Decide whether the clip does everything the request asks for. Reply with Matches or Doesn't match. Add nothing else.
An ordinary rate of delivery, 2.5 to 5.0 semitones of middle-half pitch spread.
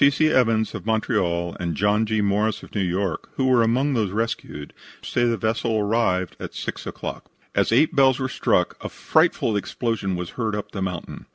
Matches